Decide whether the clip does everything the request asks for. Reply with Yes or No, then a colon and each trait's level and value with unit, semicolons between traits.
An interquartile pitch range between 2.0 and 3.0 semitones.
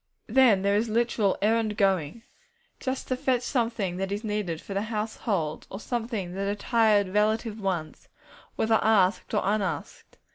Yes: narrow, 2.6 semitones